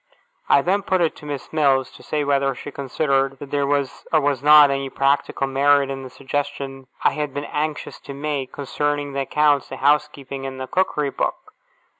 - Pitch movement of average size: No, narrow, 1.4 semitones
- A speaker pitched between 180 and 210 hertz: No, medium, 140 Hz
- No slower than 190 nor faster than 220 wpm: Yes, average, 195 wpm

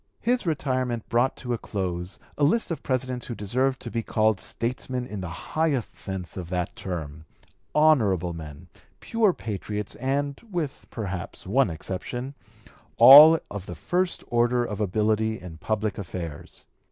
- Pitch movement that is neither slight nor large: No, wide, 6.0 semitones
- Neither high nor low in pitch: No, low, 115 Hz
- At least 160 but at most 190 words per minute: No, average, 150 wpm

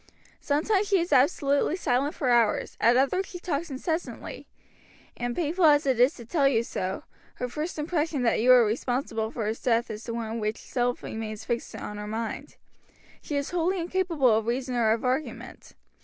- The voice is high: Yes, very high, 255 Hz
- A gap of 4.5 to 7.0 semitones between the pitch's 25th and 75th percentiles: Yes, average, 5.1 semitones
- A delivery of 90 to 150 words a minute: No, average, 185 wpm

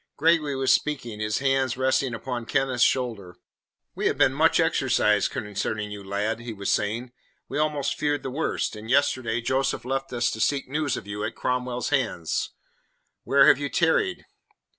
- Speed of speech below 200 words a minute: Yes, average, 170 wpm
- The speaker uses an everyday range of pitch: Yes, average, 3.8 semitones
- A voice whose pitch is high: No, low, 125 Hz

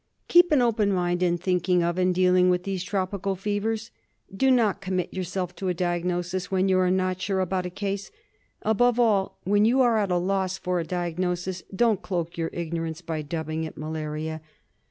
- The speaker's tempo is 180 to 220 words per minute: Yes, average, 190 wpm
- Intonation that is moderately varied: No, narrow, 2.2 semitones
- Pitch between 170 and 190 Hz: Yes, medium, 185 Hz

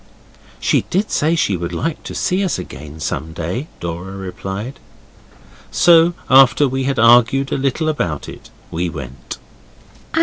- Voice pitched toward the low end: Yes, low, 120 Hz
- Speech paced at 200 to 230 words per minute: No, average, 145 wpm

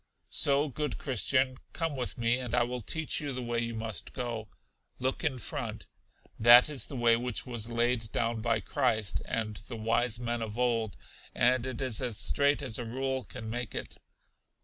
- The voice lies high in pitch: No, low, 120 Hz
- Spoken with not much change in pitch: Yes, narrow, 2.2 semitones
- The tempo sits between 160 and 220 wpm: Yes, average, 190 wpm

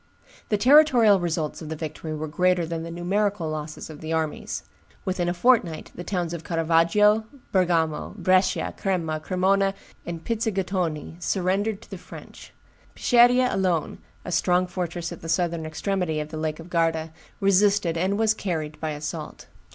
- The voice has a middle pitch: Yes, medium, 175 Hz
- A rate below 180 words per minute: Yes, average, 160 wpm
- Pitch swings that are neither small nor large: Yes, average, 3.4 semitones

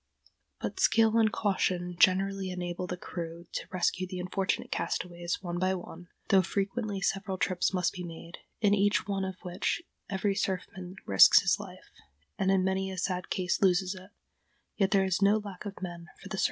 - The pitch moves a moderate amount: No, narrow, 1.6 semitones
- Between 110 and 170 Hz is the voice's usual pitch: No, high, 190 Hz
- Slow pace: No, average, 185 wpm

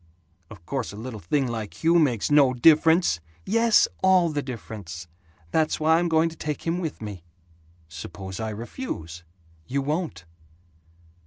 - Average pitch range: No, wide, 7.7 semitones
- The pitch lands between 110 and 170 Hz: Yes, low, 135 Hz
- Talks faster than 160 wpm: No, average, 150 wpm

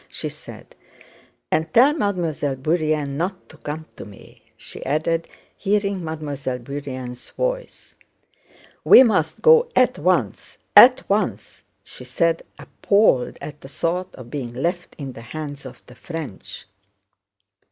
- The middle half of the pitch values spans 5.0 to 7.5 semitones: Yes, wide, 5.5 semitones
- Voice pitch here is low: No, medium, 155 Hz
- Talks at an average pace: No, slow, 130 wpm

